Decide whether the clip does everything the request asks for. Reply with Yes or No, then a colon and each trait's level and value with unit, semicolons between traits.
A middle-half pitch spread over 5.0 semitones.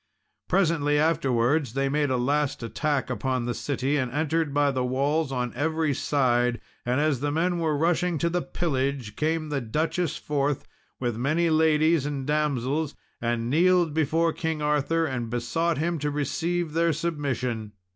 No: average, 3.7 semitones